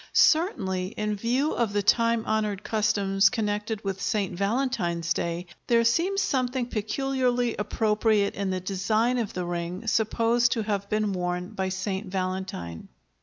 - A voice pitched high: Yes, high, 210 Hz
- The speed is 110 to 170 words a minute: Yes, average, 145 wpm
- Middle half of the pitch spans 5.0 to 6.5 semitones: No, average, 3.6 semitones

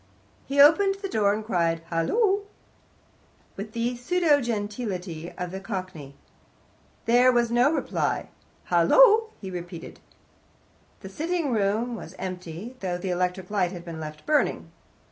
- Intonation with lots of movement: Yes, wide, 6.4 semitones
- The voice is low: No, high, 205 Hz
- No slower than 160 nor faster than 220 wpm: No, slow, 135 wpm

